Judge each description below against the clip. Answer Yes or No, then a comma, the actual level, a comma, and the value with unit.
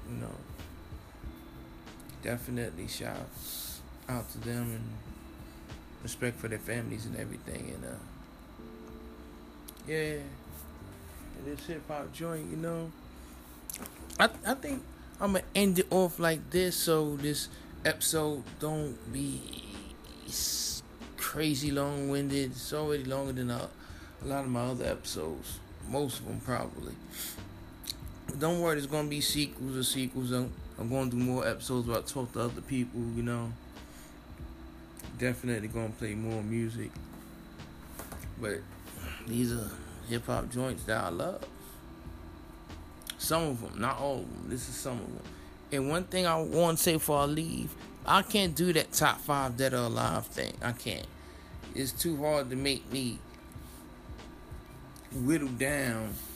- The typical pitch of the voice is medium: No, low, 120 Hz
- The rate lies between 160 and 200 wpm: No, average, 145 wpm